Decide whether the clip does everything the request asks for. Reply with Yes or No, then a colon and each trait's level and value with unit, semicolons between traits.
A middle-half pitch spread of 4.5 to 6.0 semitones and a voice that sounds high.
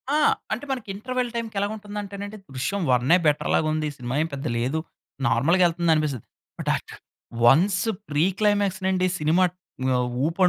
No: average, 5.3 semitones; medium, 180 Hz